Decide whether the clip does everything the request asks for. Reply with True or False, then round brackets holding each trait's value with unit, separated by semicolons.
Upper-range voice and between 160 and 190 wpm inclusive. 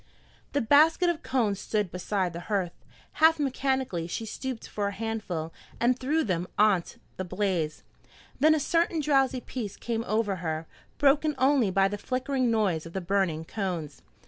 True (215 Hz; 165 wpm)